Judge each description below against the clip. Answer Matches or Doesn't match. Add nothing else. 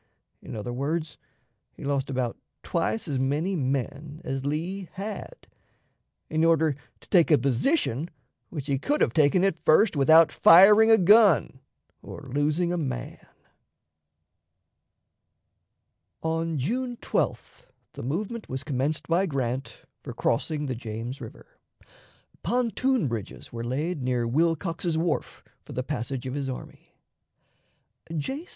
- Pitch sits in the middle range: Matches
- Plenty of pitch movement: Doesn't match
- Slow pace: Matches